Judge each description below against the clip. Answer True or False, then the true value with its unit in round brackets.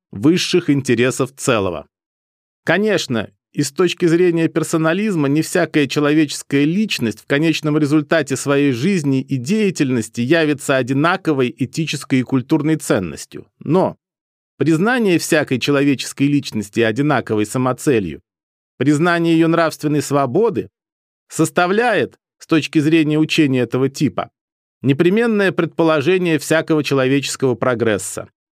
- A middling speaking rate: False (105 wpm)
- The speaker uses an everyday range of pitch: True (3.7 semitones)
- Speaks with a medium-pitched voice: True (150 Hz)